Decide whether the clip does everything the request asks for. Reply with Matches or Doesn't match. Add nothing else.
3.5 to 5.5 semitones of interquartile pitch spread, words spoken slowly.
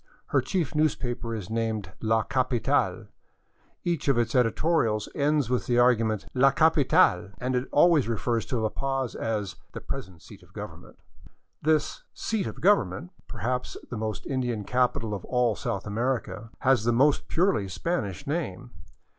Doesn't match